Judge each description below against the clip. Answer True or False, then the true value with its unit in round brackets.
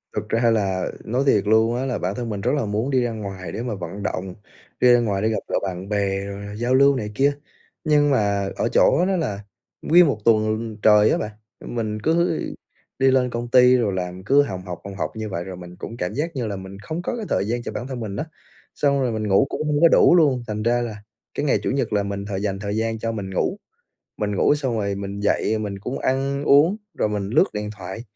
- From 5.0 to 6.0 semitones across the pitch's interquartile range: False (4.5 semitones)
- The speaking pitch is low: True (110 Hz)